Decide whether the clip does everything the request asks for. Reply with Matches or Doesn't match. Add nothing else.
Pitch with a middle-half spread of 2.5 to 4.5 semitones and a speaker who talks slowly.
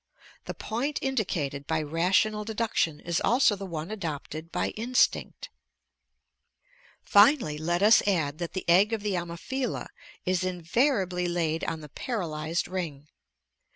Doesn't match